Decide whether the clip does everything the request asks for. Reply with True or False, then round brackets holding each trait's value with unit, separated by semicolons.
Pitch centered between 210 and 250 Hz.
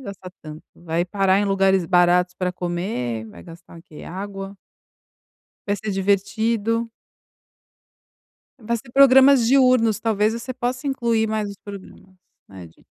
False (200 Hz)